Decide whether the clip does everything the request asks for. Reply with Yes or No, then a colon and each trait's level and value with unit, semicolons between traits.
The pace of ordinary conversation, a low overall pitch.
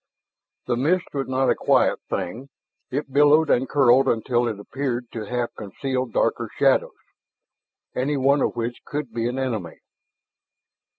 Yes: average, 145 wpm; low, 130 Hz